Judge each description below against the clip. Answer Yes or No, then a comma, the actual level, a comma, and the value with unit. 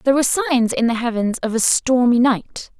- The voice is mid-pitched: No, high, 245 Hz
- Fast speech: Yes, fast, 215 wpm